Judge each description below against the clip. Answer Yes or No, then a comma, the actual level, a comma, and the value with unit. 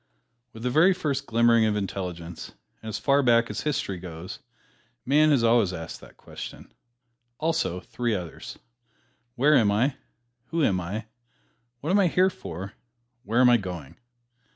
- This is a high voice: No, low, 115 Hz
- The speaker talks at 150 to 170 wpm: Yes, average, 155 wpm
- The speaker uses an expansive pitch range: Yes, wide, 6.9 semitones